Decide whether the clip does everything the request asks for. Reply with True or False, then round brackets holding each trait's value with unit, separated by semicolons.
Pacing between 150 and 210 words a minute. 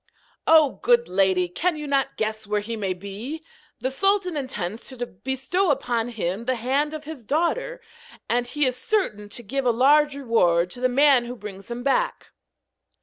True (180 wpm)